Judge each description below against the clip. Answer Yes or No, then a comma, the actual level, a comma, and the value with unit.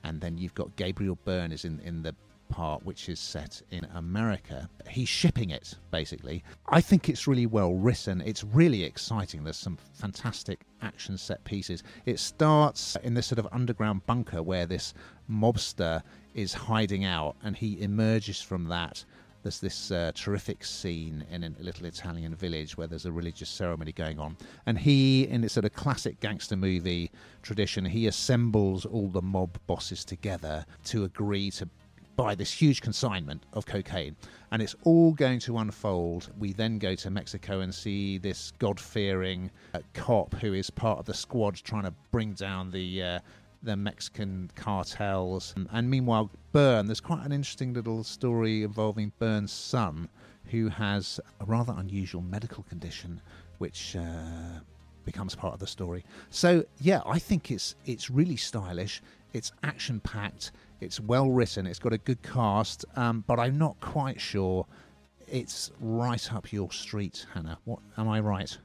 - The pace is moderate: Yes, average, 165 wpm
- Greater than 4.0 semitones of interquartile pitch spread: Yes, average, 4.4 semitones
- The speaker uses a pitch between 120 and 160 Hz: No, low, 100 Hz